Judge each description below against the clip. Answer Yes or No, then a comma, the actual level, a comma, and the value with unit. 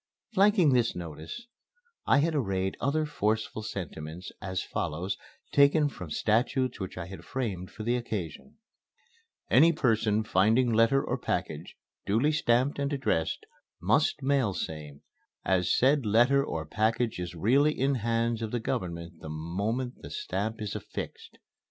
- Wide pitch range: Yes, wide, 6.5 semitones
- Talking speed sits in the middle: Yes, average, 145 wpm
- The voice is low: Yes, low, 115 Hz